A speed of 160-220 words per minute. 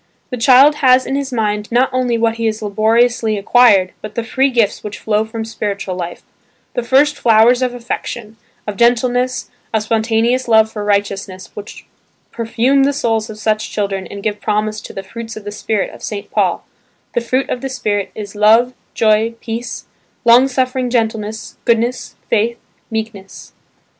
Yes: average, 170 wpm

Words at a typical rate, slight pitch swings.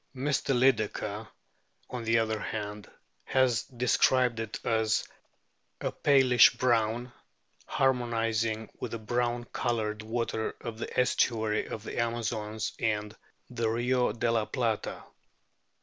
No: slow, 120 wpm; narrow, 1.9 semitones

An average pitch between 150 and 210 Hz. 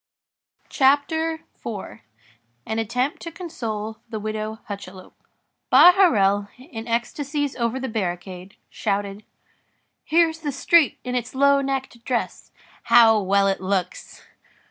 No: high, 230 Hz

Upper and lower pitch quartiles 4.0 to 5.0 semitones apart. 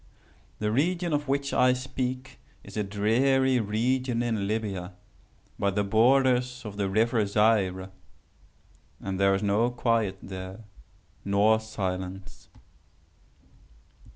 Yes: average, 4.3 semitones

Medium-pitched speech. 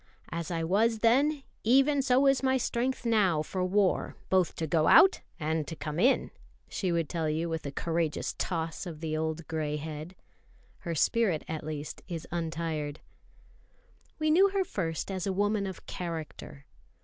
Yes: medium, 170 Hz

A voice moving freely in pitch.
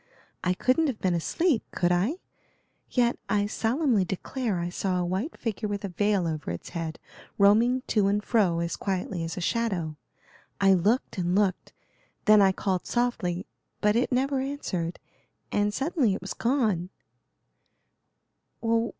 No: average, 4.9 semitones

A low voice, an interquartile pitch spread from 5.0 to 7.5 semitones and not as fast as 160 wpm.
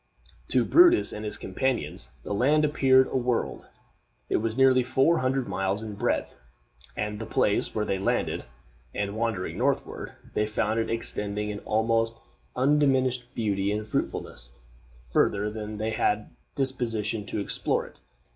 No: low, 110 Hz; average, 3.6 semitones; average, 150 wpm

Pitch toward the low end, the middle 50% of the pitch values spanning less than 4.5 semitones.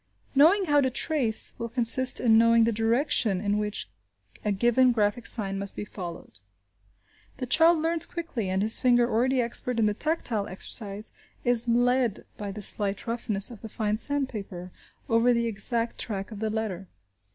No: high, 230 Hz; average, 3.3 semitones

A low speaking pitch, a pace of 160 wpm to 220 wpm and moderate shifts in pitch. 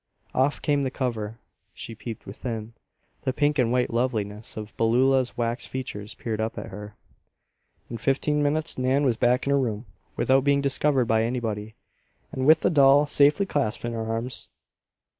Yes: low, 125 Hz; average, 170 wpm; average, 3.7 semitones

